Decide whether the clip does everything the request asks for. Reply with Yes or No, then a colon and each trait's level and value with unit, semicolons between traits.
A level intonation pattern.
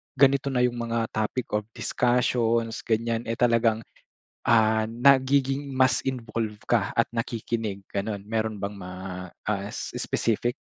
Yes: narrow, 2.2 semitones